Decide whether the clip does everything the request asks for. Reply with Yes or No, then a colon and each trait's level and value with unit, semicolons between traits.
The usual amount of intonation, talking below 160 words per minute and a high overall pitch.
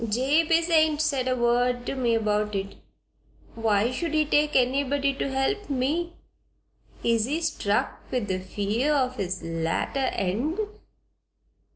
No: wide, 5.8 semitones; average, 140 wpm; very high, 255 Hz